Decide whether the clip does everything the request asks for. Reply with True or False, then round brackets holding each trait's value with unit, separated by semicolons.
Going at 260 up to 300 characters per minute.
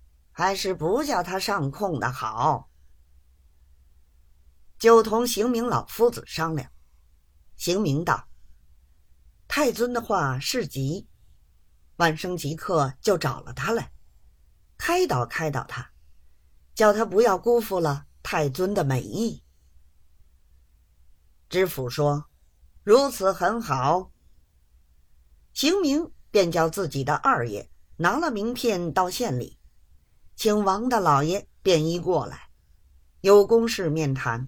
False (155 characters per minute)